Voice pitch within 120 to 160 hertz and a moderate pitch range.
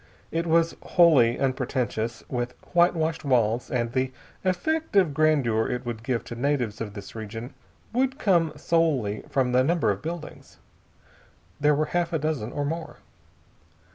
No: medium, 140 Hz; wide, 5.7 semitones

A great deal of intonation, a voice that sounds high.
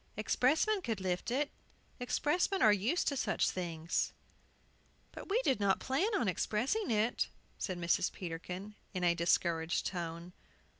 Yes: wide, 7.3 semitones; high, 205 Hz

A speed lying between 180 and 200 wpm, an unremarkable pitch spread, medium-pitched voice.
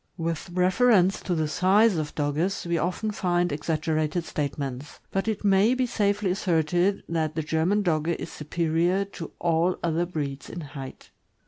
No: average, 155 wpm; average, 3.6 semitones; medium, 170 Hz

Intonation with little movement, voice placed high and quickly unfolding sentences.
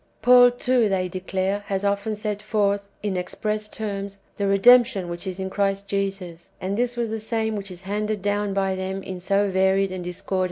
Yes: narrow, 1.9 semitones; high, 200 Hz; fast, 210 wpm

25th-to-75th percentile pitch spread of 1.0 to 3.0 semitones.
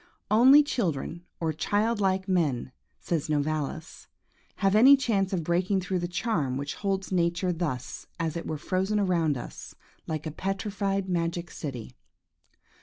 No: average, 3.8 semitones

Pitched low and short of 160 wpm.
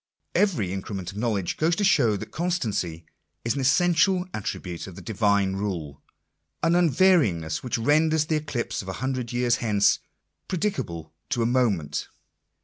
Yes: low, 115 Hz; average, 150 wpm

